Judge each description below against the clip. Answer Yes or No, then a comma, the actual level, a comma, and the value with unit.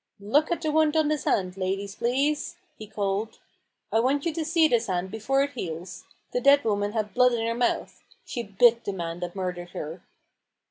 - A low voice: No, high, 225 Hz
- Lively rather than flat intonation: Yes, wide, 6.4 semitones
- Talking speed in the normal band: No, fast, 220 wpm